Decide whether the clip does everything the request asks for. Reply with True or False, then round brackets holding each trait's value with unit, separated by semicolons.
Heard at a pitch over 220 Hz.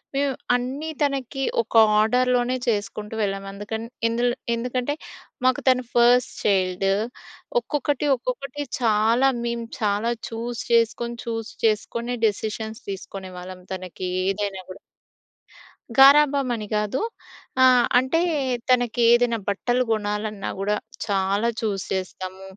True (230 Hz)